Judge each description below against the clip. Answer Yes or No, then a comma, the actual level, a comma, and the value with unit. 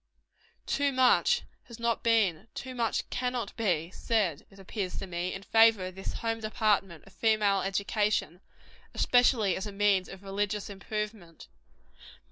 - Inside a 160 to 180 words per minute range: No, average, 145 wpm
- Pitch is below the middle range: No, high, 205 Hz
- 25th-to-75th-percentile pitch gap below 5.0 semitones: Yes, average, 2.9 semitones